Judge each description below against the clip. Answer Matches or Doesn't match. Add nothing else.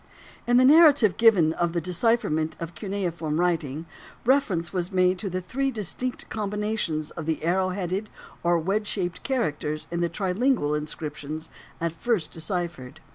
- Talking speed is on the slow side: Doesn't match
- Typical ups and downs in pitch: Matches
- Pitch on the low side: Doesn't match